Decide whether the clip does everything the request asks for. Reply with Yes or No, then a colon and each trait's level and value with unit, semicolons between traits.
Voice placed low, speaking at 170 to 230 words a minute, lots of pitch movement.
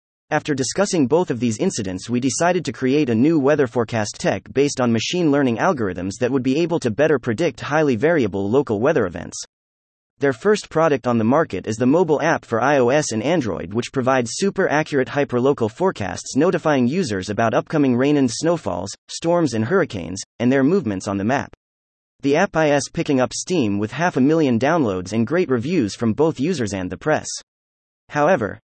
Yes: low, 130 Hz; average, 185 wpm; wide, 6.1 semitones